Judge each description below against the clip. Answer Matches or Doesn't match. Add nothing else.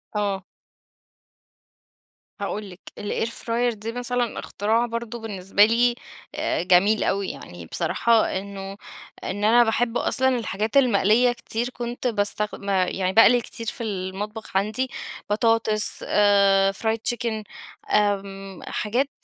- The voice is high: Matches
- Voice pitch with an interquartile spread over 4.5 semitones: Doesn't match